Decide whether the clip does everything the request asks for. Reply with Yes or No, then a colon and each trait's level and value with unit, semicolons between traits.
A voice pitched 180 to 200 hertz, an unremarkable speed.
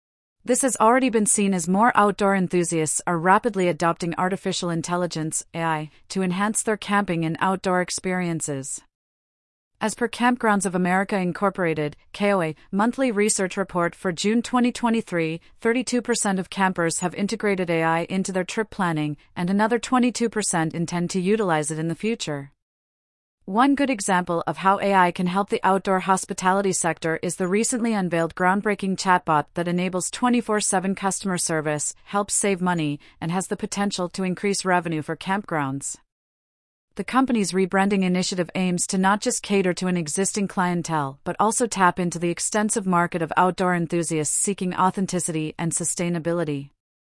Yes: medium, 185 Hz; average, 150 wpm